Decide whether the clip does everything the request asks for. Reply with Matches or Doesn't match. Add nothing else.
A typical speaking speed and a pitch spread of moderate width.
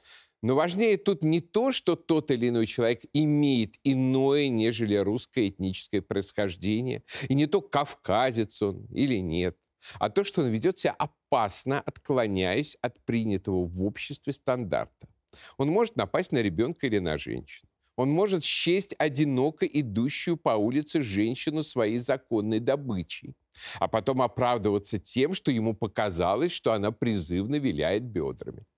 Doesn't match